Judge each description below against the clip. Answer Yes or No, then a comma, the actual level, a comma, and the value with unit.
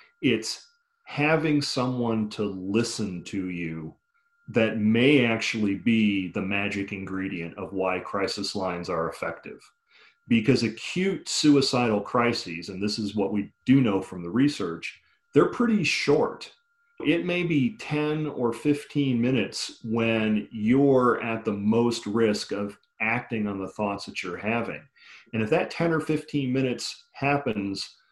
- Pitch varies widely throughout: Yes, wide, 5.9 semitones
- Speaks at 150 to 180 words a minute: No, average, 140 wpm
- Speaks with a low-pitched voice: Yes, low, 115 Hz